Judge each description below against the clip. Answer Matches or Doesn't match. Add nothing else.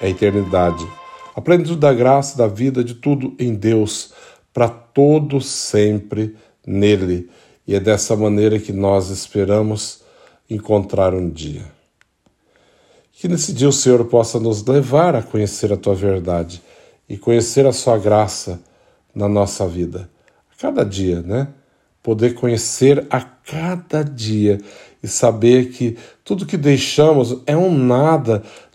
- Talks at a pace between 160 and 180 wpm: Doesn't match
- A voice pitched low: Matches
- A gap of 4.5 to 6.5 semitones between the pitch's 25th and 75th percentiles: Matches